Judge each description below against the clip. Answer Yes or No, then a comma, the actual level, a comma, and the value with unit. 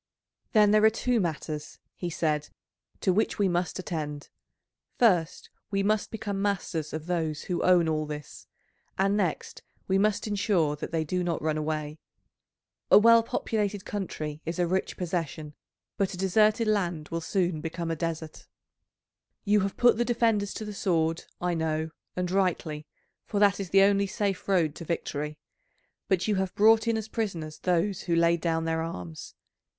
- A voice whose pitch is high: No, medium, 180 Hz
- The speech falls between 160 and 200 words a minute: Yes, average, 170 wpm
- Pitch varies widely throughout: No, average, 4.1 semitones